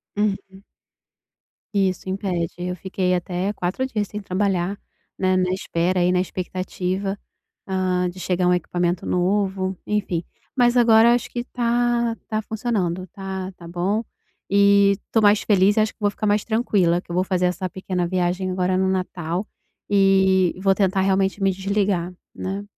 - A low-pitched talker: No, high, 190 Hz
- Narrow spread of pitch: Yes, narrow, 2.0 semitones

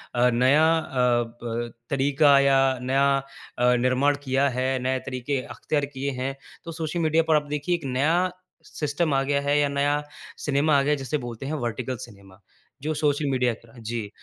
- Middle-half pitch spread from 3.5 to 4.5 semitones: No, narrow, 2.6 semitones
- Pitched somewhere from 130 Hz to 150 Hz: Yes, medium, 140 Hz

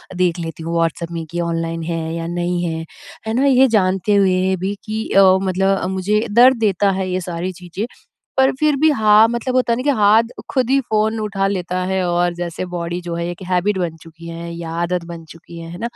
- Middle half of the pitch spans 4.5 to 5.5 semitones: No, average, 3.8 semitones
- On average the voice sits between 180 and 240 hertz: Yes, medium, 185 Hz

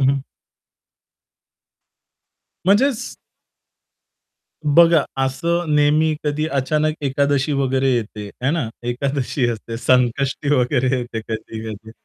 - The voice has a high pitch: No, low, 135 Hz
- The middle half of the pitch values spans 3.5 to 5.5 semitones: Yes, average, 3.9 semitones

